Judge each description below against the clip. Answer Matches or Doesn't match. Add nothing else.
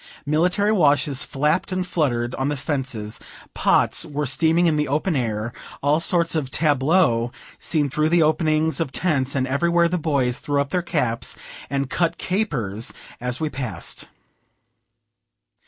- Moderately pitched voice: Matches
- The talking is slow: Doesn't match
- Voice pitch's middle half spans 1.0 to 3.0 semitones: Doesn't match